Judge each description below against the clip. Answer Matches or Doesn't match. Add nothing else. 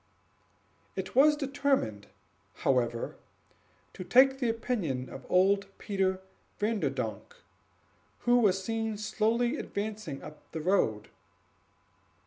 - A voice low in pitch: Doesn't match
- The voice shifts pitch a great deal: Matches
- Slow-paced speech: Matches